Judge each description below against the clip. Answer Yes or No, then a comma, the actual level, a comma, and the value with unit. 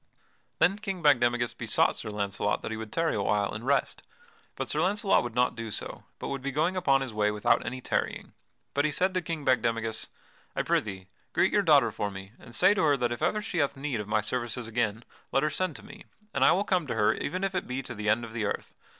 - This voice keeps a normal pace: No, fast, 245 wpm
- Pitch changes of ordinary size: No, wide, 6.2 semitones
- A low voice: Yes, low, 125 Hz